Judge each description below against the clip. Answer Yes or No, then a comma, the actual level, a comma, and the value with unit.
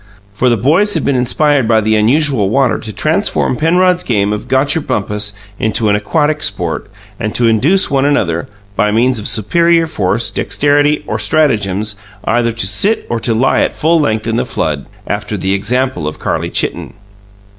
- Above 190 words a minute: No, average, 175 wpm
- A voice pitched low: Yes, low, 120 Hz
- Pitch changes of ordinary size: No, wide, 5.9 semitones